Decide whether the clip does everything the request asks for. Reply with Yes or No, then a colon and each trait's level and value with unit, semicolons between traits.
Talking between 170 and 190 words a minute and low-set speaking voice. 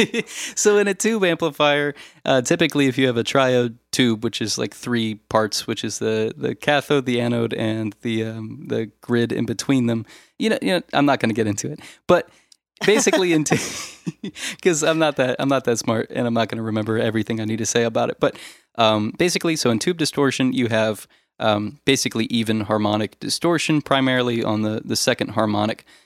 No: fast, 205 wpm; low, 120 Hz